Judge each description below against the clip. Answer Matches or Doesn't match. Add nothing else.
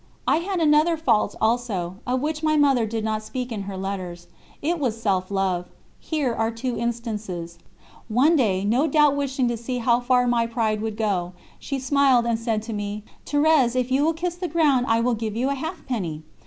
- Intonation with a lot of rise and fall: Doesn't match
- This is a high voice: Matches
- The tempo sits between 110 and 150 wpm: Doesn't match